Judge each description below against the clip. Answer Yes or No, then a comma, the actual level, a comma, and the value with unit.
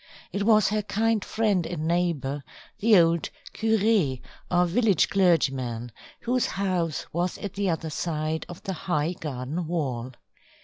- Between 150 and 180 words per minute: No, average, 140 wpm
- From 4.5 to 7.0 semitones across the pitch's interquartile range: Yes, average, 4.8 semitones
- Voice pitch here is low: No, medium, 175 Hz